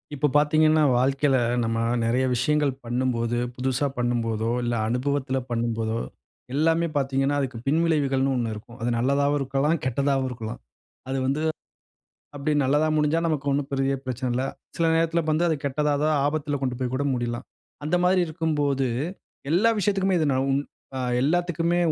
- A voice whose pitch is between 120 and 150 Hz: Yes, medium, 140 Hz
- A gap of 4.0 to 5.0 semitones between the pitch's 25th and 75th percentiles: No, average, 3.4 semitones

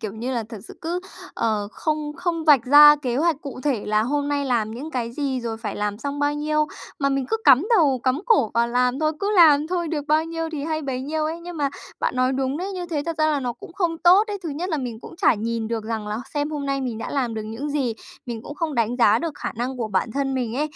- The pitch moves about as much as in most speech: Yes, average, 4.7 semitones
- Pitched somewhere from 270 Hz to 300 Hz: Yes, very high, 280 Hz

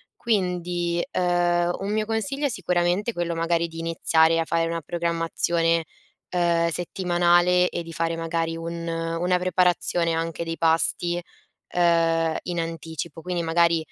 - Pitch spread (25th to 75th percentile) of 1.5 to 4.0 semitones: No, narrow, 1.1 semitones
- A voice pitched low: No, medium, 170 Hz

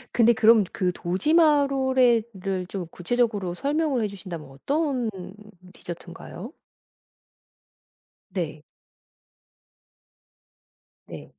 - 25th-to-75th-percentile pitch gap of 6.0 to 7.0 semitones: Yes, wide, 6.6 semitones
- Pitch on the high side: Yes, high, 220 Hz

